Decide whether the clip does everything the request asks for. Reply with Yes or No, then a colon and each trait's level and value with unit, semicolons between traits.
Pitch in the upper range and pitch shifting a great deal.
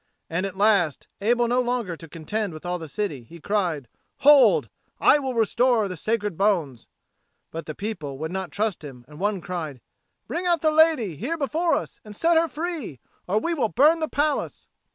Yes: high, 210 Hz; wide, 8.2 semitones